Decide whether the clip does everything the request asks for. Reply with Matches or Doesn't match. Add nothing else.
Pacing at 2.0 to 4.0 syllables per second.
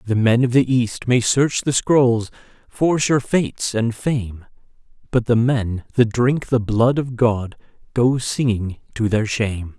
Matches